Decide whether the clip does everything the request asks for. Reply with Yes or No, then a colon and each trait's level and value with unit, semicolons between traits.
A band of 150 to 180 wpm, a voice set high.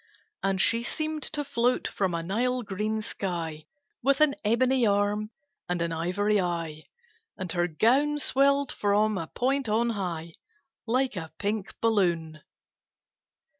No: slow, 135 wpm; high, 210 Hz